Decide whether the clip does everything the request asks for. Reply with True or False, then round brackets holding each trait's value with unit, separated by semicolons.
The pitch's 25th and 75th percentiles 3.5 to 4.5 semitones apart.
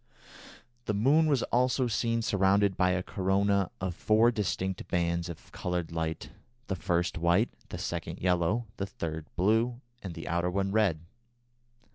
True (4.0 semitones)